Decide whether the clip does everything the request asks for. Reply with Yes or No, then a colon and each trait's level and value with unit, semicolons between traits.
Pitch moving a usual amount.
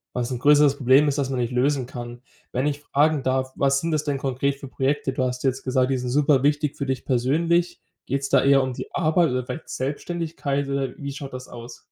No: narrow, 2.2 semitones